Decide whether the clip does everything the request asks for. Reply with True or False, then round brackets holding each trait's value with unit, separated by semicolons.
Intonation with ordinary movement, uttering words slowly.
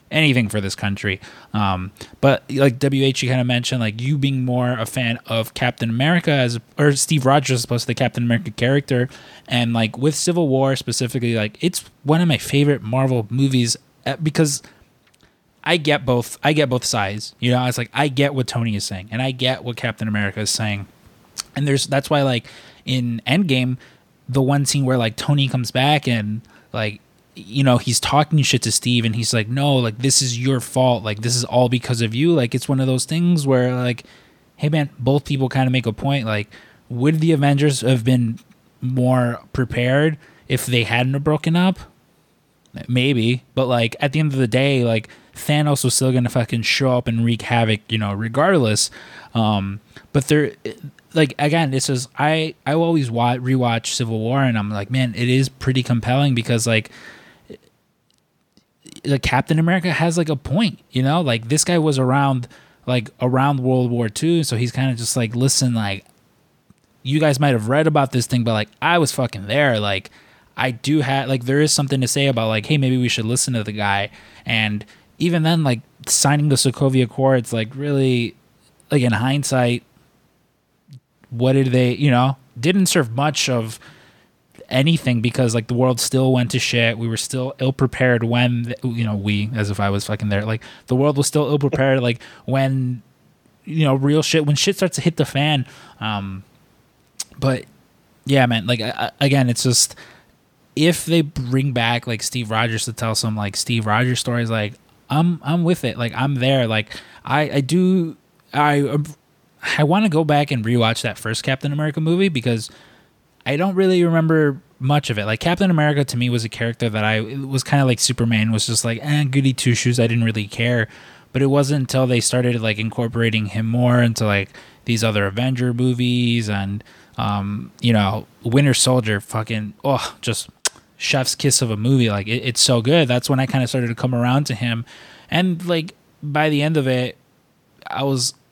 False (3.4 semitones; 200 wpm)